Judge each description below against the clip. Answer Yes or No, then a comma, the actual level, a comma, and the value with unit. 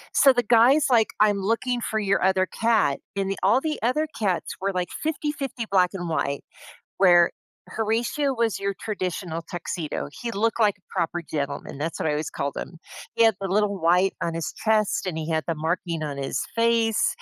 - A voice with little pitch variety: No, average, 5.2 semitones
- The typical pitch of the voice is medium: No, high, 195 Hz